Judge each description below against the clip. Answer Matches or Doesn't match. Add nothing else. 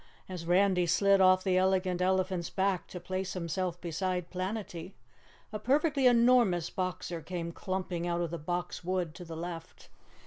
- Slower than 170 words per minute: Matches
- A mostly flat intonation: Matches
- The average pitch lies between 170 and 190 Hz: Matches